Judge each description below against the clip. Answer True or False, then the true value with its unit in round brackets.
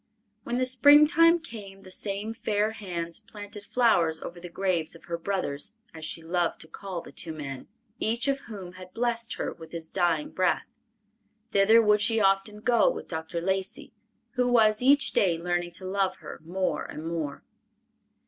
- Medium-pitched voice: False (195 Hz)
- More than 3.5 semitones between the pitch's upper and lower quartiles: True (4.8 semitones)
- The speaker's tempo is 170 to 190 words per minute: True (175 wpm)